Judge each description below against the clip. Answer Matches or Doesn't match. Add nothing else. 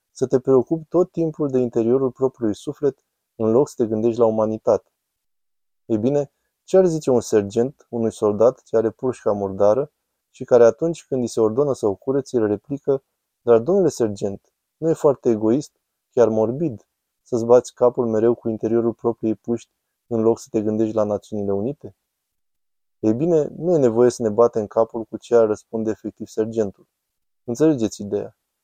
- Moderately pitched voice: Doesn't match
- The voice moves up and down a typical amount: Matches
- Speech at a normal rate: Doesn't match